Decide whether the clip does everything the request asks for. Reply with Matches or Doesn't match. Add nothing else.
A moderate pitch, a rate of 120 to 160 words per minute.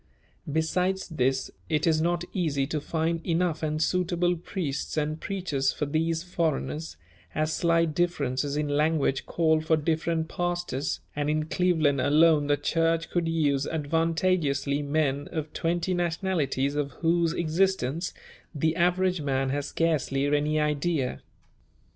Matches